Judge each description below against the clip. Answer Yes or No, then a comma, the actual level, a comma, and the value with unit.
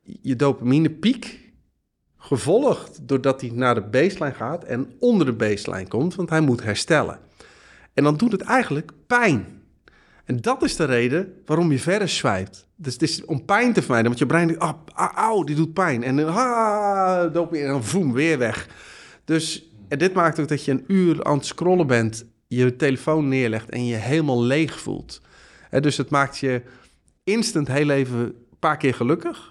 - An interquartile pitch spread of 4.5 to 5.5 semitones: Yes, average, 5.2 semitones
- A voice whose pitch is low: No, medium, 150 Hz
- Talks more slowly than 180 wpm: No, average, 185 wpm